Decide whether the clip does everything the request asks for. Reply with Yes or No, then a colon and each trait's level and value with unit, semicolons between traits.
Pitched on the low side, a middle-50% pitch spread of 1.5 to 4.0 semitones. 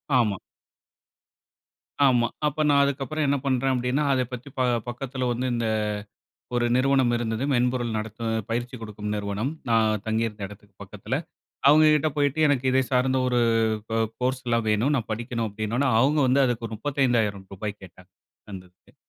Yes: low, 120 Hz; average, 3.3 semitones